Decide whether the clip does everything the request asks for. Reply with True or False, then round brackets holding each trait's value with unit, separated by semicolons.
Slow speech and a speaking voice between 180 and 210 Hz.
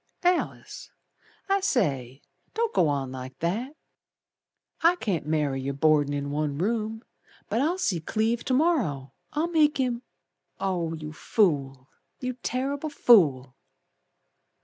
True (130 wpm; 190 Hz)